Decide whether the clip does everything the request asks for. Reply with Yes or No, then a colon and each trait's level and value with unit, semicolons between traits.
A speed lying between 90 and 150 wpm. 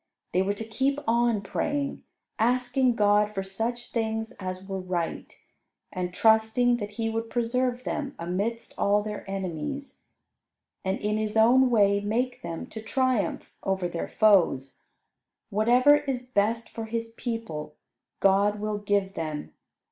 Yes: average, 140 wpm